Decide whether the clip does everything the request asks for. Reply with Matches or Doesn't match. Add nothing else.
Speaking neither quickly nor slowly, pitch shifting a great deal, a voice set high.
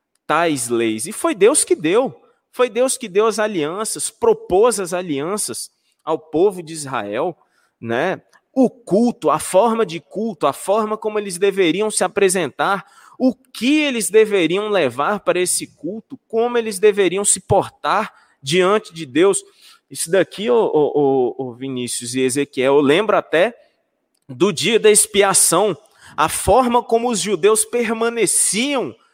Matches